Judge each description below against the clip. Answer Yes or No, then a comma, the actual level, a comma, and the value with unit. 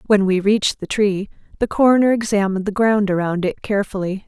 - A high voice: Yes, high, 205 Hz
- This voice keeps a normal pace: Yes, average, 180 wpm